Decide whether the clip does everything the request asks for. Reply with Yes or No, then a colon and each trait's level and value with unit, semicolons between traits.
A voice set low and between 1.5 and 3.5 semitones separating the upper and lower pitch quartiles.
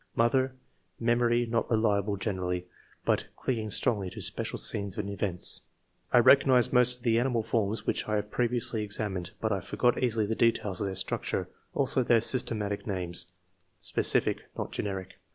Yes: low, 110 Hz; average, 3.2 semitones